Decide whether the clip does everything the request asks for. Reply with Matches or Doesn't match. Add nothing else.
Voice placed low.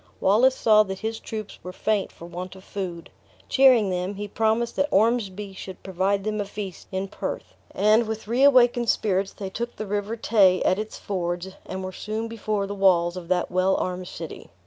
Doesn't match